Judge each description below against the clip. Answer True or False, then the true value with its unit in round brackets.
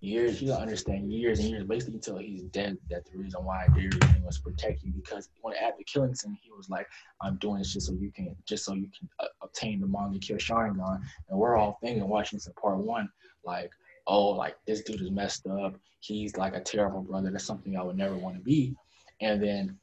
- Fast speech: True (235 wpm)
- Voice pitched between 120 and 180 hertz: False (100 Hz)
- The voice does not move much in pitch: True (2.3 semitones)